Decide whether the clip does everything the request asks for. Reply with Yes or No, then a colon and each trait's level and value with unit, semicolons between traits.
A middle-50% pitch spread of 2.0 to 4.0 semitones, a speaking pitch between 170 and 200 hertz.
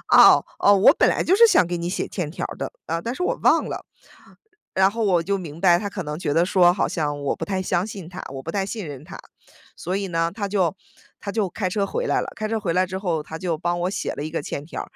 Yes: average, 3.2 semitones; medium, 185 Hz